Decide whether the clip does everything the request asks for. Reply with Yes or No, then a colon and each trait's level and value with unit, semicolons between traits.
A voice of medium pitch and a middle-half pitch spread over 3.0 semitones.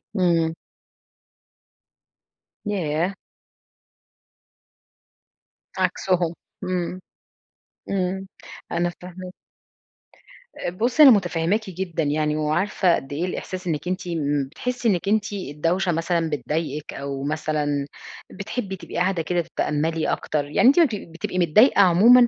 Yes: medium, 175 Hz; average, 3.6 semitones